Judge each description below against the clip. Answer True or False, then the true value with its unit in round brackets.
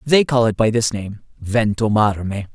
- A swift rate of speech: False (140 wpm)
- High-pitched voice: False (110 Hz)